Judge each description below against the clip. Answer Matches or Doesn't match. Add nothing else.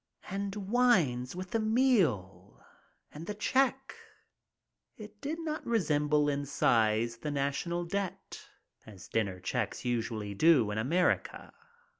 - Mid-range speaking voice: Matches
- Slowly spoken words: Matches